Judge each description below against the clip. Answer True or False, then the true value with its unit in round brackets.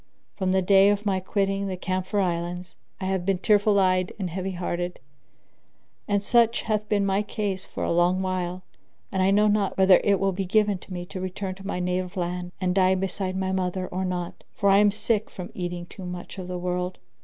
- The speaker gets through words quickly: True (210 wpm)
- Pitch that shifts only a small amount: True (1.6 semitones)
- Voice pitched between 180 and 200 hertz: True (190 Hz)